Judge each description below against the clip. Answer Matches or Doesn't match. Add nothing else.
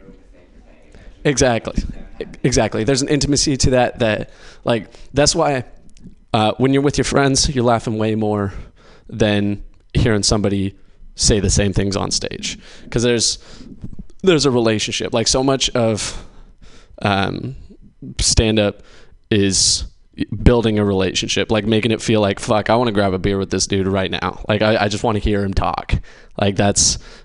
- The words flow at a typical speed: Matches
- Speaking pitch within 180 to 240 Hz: Doesn't match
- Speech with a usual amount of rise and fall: Matches